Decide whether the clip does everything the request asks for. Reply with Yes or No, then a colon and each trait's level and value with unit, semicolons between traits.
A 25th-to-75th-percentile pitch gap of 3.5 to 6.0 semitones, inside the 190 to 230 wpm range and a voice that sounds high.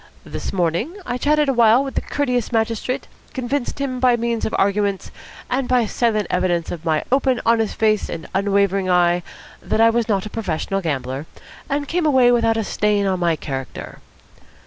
No: average, 5.0 semitones; average, 180 wpm; high, 220 Hz